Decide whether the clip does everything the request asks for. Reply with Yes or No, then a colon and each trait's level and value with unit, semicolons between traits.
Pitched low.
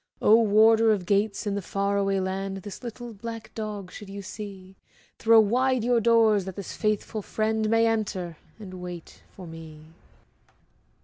No: high, 205 Hz